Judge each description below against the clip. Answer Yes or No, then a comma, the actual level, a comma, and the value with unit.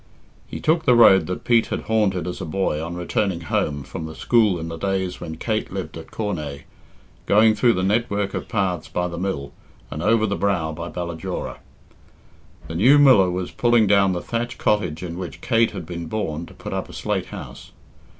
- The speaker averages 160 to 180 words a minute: No, average, 200 wpm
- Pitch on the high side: No, very low, 95 Hz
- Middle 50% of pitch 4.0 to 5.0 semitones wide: Yes, average, 4.3 semitones